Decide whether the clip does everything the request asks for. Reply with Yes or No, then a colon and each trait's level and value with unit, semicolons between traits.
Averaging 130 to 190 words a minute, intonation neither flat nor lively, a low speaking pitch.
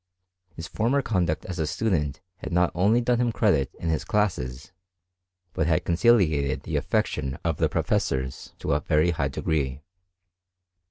No: average, 155 wpm; wide, 6.3 semitones; very low, 85 Hz